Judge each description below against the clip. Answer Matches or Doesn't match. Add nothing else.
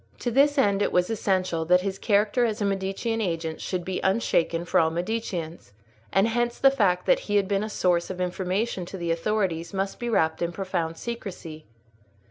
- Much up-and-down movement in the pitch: Doesn't match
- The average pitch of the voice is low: Doesn't match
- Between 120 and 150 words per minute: Doesn't match